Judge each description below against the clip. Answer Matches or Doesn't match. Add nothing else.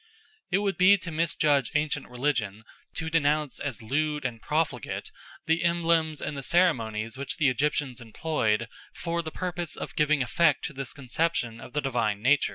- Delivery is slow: Doesn't match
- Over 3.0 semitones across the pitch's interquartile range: Matches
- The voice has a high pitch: Doesn't match